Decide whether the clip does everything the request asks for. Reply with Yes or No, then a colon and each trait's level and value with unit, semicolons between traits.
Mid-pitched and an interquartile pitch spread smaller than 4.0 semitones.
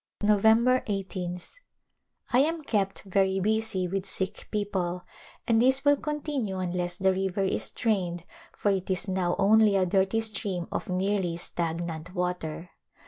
No: high, 195 Hz; average, 3.3 semitones